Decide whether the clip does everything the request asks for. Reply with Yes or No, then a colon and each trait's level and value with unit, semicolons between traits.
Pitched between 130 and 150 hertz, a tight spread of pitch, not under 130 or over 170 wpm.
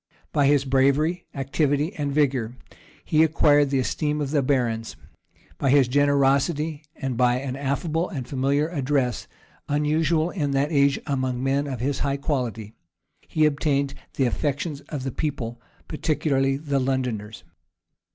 Yes: medium, 140 Hz; narrow, 2.1 semitones; average, 145 wpm